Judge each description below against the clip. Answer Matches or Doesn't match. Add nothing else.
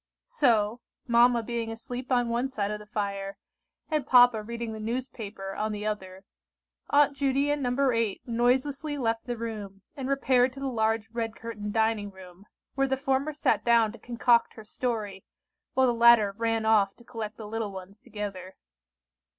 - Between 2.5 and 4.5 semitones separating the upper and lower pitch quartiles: Matches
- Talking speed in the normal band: Matches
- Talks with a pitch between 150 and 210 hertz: Doesn't match